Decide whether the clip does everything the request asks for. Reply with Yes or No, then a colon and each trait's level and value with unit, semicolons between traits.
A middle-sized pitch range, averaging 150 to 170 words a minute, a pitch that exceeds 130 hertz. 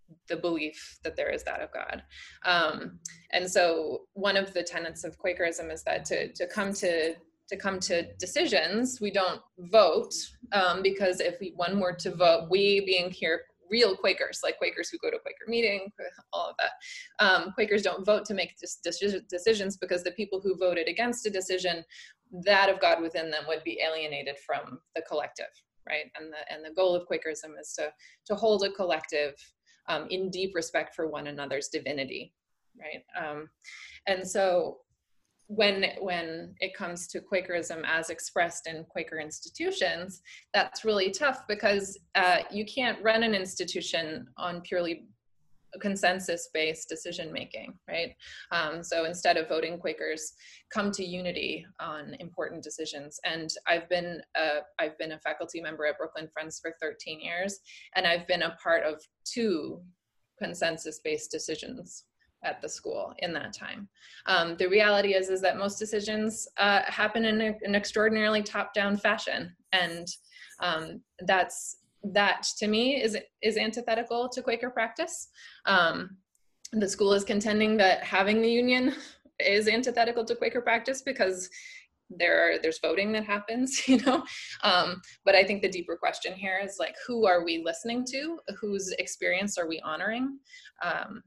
Yes: average, 4.3 semitones; average, 160 wpm; high, 190 Hz